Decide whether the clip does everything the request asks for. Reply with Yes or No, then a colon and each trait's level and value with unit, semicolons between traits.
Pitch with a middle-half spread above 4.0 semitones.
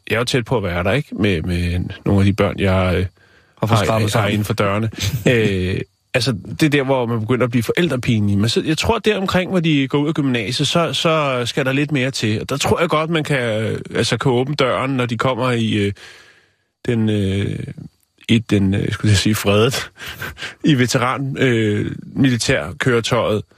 Yes: average, 4.7 semitones